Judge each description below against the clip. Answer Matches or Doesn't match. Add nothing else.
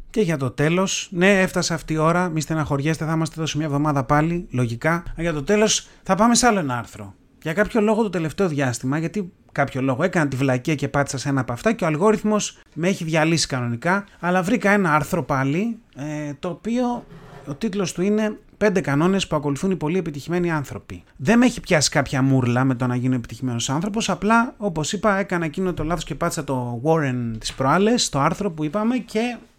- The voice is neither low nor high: Matches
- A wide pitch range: Matches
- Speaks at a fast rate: Matches